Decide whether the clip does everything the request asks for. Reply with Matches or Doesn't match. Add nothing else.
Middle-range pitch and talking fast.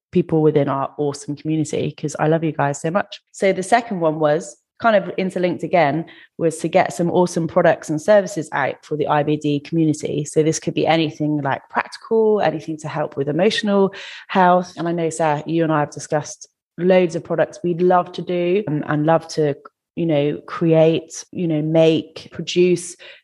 Doesn't match